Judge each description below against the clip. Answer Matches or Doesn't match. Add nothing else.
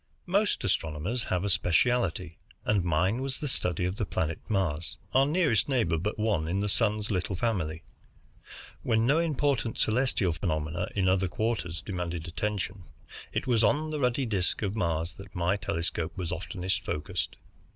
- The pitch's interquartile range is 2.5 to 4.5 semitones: Doesn't match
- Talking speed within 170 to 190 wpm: Doesn't match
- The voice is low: Matches